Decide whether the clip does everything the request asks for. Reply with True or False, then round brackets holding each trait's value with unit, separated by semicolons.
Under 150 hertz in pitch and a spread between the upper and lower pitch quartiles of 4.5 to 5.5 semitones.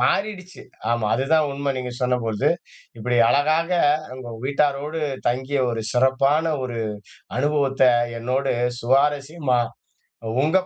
False (140 Hz; 3.3 semitones)